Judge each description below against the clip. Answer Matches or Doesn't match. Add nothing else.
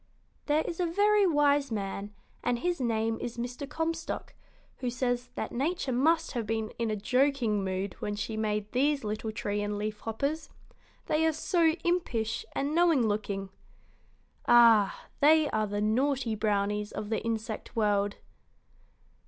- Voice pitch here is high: Matches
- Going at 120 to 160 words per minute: Matches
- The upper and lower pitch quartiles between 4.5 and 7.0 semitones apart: Matches